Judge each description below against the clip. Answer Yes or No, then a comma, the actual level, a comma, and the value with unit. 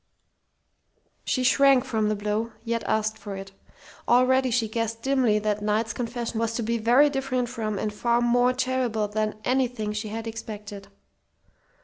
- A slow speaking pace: No, average, 155 wpm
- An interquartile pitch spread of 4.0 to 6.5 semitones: No, average, 2.7 semitones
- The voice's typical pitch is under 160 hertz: No, high, 230 Hz